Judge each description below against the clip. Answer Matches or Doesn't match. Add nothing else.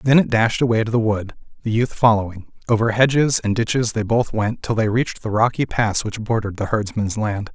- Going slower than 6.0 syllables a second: Matches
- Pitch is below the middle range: Matches